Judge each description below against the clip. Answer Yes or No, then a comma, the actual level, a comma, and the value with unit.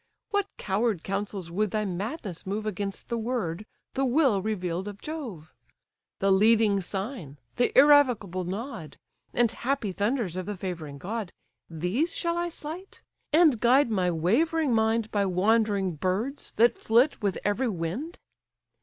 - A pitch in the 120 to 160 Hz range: No, high, 215 Hz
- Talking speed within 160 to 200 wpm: No, average, 145 wpm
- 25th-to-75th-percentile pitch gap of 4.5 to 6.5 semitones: Yes, average, 5.1 semitones